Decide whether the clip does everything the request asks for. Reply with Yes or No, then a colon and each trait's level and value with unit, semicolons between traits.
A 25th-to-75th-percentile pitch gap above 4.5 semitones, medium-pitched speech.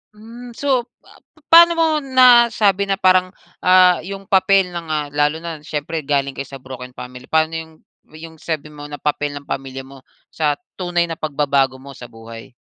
Yes: wide, 5.6 semitones; medium, 160 Hz